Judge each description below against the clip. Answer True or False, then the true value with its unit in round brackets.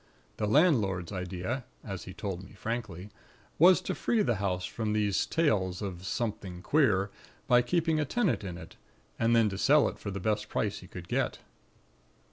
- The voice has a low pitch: True (105 Hz)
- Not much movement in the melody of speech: False (4.6 semitones)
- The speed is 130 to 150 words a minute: False (180 wpm)